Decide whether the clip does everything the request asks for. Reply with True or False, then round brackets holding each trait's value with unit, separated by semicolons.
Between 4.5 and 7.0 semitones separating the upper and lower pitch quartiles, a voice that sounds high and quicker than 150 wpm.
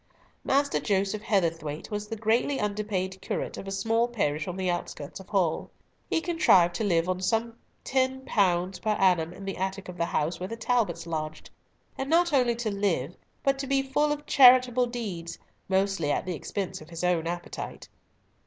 True (5.4 semitones; 195 Hz; 180 wpm)